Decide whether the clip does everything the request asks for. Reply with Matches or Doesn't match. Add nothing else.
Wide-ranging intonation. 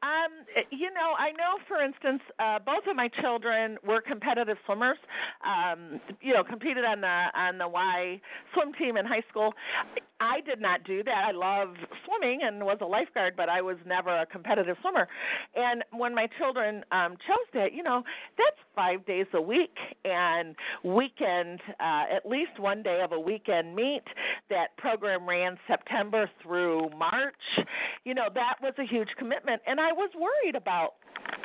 Matches